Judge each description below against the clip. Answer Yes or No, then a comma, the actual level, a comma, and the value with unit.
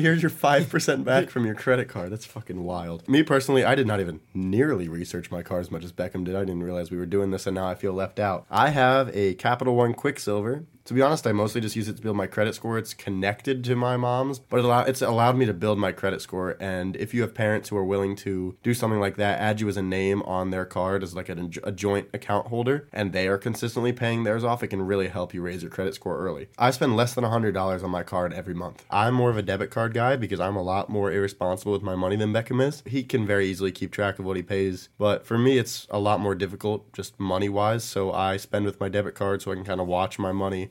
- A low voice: Yes, low, 100 Hz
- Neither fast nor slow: No, fast, 265 wpm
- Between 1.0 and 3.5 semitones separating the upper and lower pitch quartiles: No, average, 4.1 semitones